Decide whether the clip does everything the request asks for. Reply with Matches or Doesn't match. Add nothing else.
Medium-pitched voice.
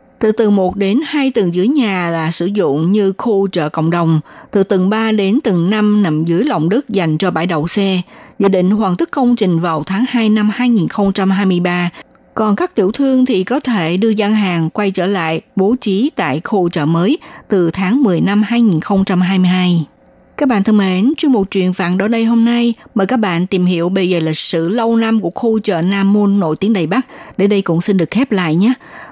Doesn't match